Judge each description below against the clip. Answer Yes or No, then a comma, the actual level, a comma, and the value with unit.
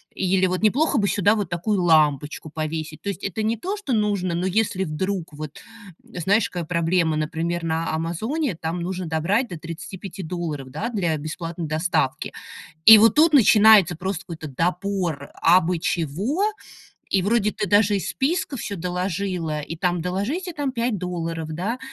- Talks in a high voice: No, medium, 180 Hz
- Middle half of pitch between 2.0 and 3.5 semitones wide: No, average, 4.0 semitones